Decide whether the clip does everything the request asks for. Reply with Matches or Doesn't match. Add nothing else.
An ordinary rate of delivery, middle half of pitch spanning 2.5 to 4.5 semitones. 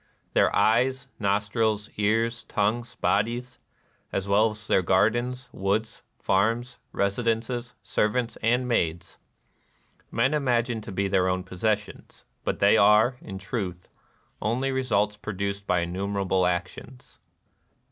Doesn't match